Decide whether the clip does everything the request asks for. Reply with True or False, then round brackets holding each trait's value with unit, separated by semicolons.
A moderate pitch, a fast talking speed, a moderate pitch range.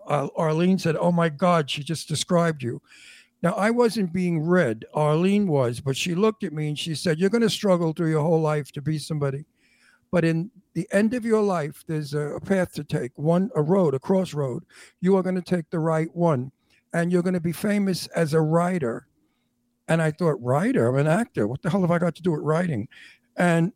True (165 Hz; 220 wpm; 3.4 semitones)